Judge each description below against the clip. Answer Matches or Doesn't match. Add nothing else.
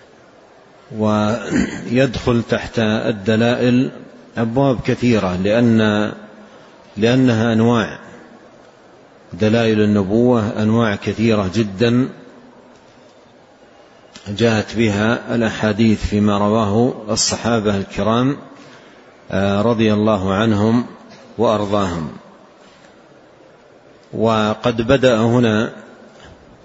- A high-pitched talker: Doesn't match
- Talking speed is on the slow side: Matches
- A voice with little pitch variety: Matches